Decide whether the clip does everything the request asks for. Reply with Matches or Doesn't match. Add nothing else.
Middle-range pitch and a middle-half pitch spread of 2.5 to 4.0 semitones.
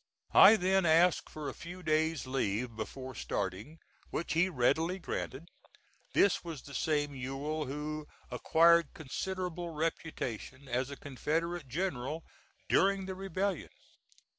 Doesn't match